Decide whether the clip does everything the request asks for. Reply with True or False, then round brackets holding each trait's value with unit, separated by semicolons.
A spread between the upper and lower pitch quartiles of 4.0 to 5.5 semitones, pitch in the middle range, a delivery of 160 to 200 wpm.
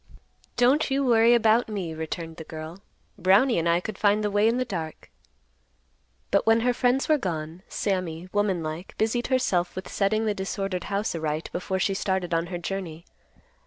False (4.8 semitones; 195 Hz; 175 wpm)